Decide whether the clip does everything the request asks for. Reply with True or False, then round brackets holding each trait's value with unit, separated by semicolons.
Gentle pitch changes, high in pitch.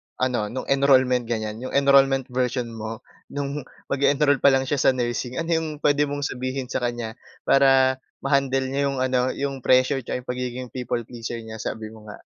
False (2.1 semitones; 130 Hz)